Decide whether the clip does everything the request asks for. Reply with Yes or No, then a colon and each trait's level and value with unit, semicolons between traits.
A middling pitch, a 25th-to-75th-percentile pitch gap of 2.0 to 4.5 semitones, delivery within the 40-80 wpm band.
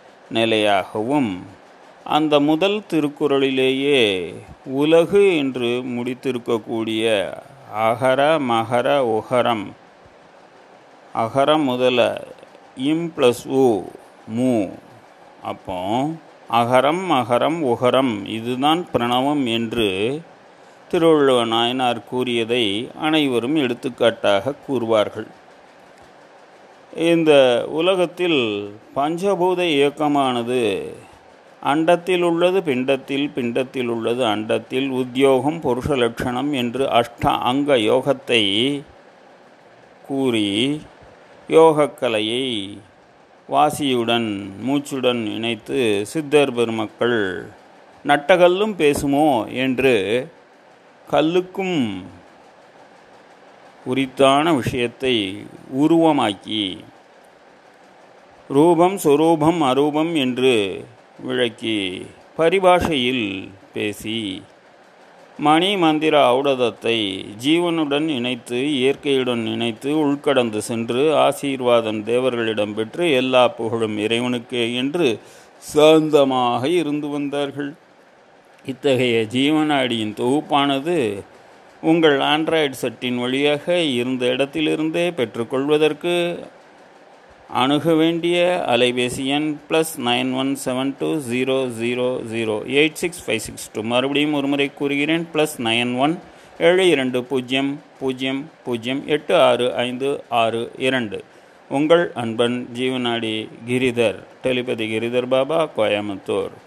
No: low, 130 Hz; average, 3.9 semitones; slow, 75 wpm